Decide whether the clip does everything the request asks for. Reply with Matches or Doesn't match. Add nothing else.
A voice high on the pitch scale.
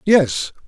Doesn't match